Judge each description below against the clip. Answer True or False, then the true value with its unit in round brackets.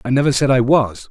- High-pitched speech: False (125 Hz)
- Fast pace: True (270 wpm)